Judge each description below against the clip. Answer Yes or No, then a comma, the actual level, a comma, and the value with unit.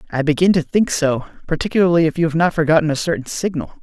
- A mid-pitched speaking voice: Yes, medium, 160 Hz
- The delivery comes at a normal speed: No, fast, 220 wpm